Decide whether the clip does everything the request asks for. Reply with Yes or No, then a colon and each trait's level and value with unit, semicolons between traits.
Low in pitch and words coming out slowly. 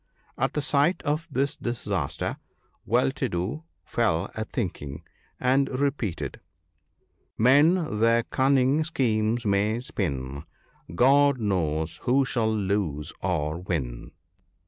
Yes: low, 110 Hz; slow, 120 wpm